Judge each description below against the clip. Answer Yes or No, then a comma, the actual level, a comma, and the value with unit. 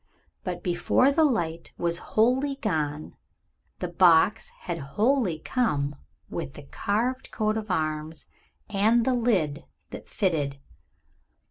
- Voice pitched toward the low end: No, medium, 185 Hz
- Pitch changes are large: Yes, wide, 6.5 semitones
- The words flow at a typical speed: No, slow, 120 wpm